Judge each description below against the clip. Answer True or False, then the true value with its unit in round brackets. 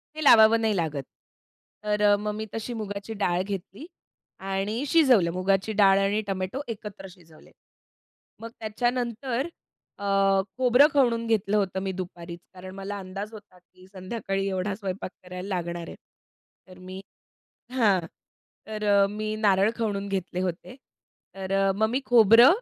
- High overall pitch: True (200 Hz)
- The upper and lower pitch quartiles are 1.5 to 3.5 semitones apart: True (3.0 semitones)